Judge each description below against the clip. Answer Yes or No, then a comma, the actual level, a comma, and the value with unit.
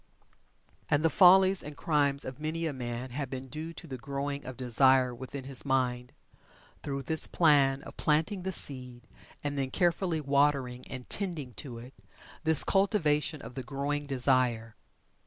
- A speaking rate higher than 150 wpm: Yes, average, 160 wpm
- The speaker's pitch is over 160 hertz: No, medium, 140 Hz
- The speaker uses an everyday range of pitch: Yes, average, 3.2 semitones